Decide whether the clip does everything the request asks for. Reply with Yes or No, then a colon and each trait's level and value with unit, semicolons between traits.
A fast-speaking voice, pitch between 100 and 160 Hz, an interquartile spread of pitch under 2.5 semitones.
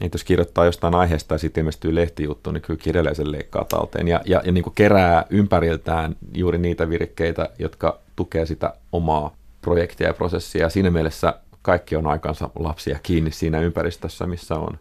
No: fast, 170 wpm; very low, 85 Hz; narrow, 2.0 semitones